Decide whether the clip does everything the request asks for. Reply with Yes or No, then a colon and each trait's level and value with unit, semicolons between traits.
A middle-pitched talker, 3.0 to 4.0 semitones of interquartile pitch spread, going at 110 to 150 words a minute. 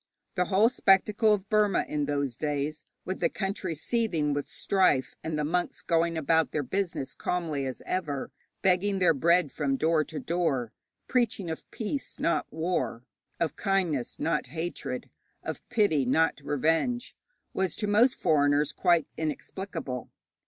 No: medium, 165 Hz; average, 4.6 semitones; average, 145 wpm